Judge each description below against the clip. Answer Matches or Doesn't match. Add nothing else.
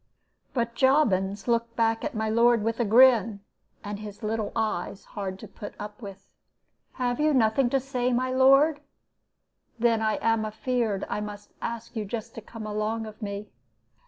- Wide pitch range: Doesn't match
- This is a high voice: Matches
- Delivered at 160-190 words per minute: Matches